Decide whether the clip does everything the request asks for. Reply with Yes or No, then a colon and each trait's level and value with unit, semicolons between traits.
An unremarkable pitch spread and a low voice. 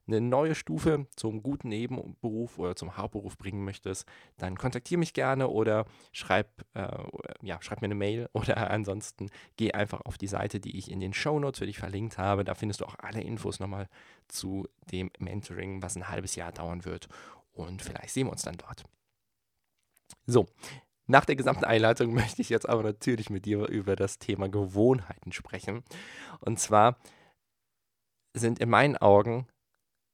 Yes: average, 3.5 semitones; low, 105 Hz